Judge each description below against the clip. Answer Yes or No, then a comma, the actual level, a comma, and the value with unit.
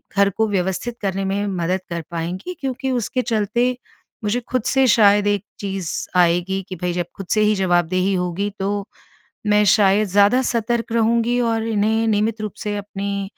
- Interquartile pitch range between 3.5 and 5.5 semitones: No, average, 2.8 semitones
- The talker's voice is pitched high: Yes, high, 205 Hz